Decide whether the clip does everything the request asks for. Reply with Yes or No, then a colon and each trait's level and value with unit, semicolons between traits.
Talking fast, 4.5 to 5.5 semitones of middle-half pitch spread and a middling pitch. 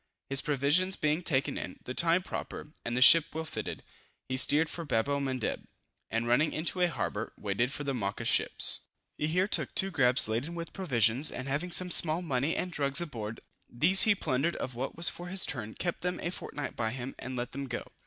Yes: fast, 210 wpm; average, 5.1 semitones; medium, 145 Hz